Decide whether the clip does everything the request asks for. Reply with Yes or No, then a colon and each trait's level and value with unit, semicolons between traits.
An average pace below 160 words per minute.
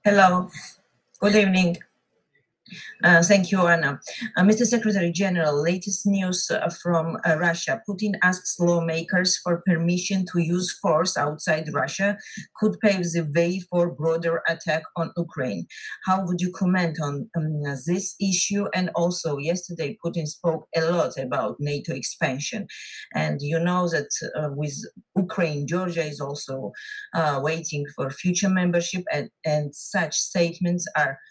Yes: average, 140 wpm